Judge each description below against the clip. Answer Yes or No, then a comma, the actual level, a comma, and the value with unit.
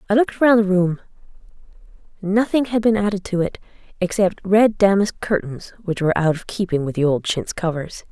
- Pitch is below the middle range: No, high, 190 Hz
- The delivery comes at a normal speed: Yes, average, 185 wpm